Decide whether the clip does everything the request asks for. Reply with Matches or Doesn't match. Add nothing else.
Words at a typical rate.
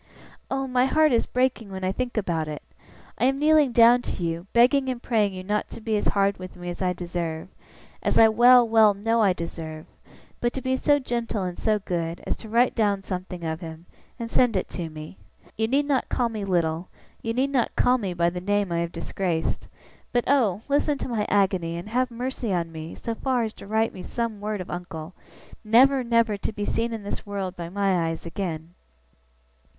Doesn't match